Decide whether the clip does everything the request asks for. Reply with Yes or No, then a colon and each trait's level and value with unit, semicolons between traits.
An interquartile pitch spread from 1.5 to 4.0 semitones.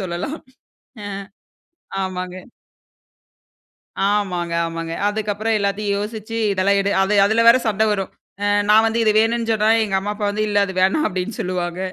Yes: narrow, 2.6 semitones